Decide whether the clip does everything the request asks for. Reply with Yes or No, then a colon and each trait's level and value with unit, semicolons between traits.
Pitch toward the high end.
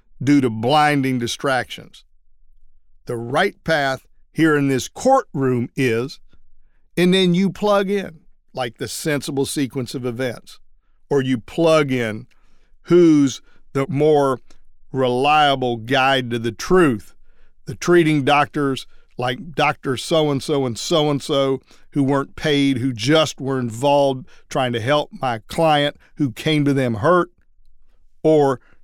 No: medium, 140 Hz